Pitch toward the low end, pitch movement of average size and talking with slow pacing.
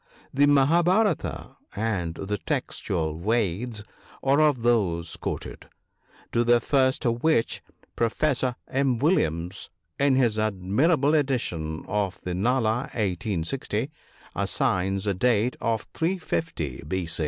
No: low, 115 Hz; wide, 6.0 semitones; slow, 120 wpm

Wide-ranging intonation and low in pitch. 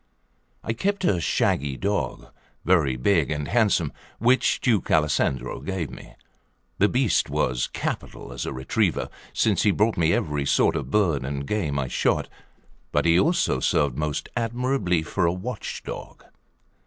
Yes: wide, 7.1 semitones; very low, 85 Hz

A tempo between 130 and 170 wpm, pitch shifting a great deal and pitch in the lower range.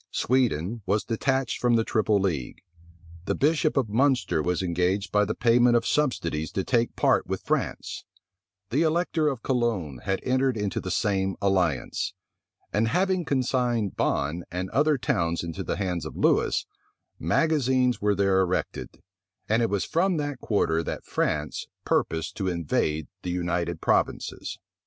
Yes: average, 150 wpm; wide, 6.4 semitones; low, 105 Hz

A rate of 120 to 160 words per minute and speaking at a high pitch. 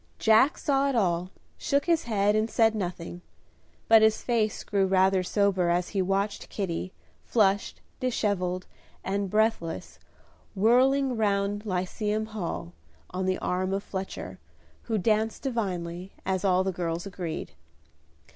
Yes: slow, 135 wpm; high, 200 Hz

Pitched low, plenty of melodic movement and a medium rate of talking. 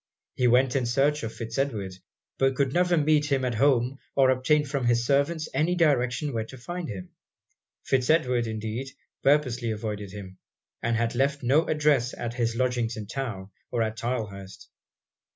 No: low, 125 Hz; average, 3.7 semitones; average, 170 wpm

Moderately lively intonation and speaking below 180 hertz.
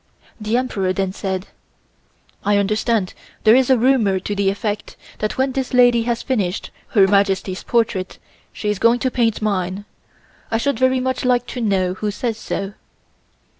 No: average, 3.9 semitones; high, 215 Hz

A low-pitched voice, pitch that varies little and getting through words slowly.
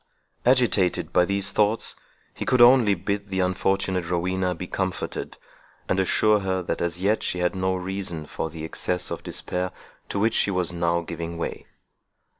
No: very low, 95 Hz; narrow, 2.1 semitones; average, 170 wpm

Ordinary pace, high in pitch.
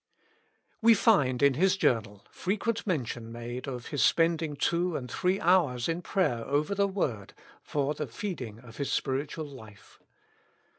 No: average, 150 wpm; medium, 145 Hz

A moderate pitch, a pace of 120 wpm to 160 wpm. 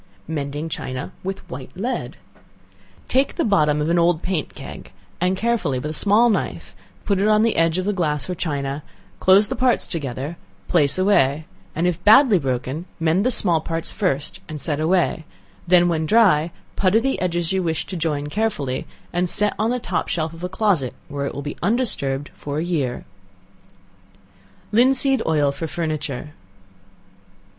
No: medium, 170 Hz; average, 170 wpm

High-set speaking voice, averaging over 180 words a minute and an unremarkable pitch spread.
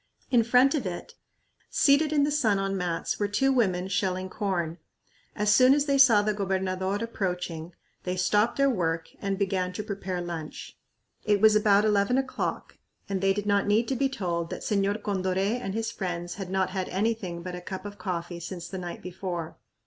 Yes: high, 195 Hz; average, 195 wpm; average, 3.1 semitones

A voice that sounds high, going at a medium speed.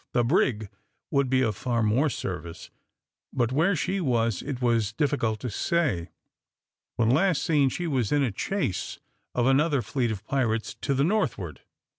No: low, 125 Hz; average, 165 wpm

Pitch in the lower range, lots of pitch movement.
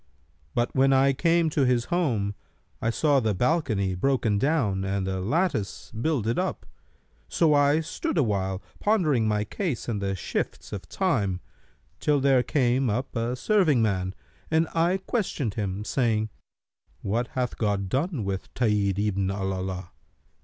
Yes: low, 120 Hz; wide, 6.7 semitones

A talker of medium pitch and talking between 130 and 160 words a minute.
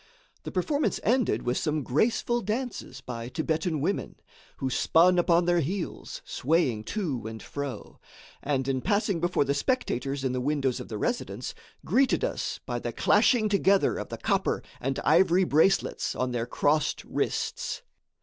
Yes: medium, 155 Hz; average, 155 wpm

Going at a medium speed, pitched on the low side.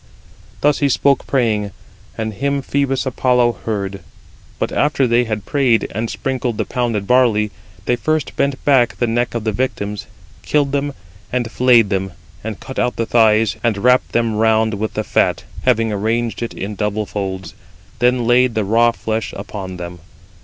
Yes: average, 170 wpm; low, 115 Hz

